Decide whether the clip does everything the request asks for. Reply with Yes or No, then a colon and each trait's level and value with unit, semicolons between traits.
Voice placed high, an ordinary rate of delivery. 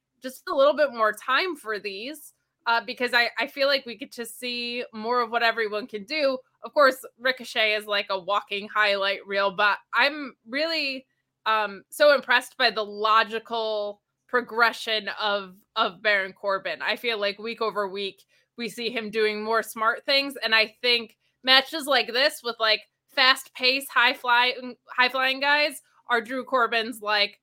Yes: high, 230 Hz; average, 170 wpm